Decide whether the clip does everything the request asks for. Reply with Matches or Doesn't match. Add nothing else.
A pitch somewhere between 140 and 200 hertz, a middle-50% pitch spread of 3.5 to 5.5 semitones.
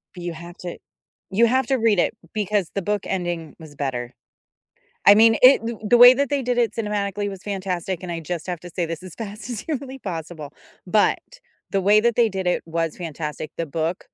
Matches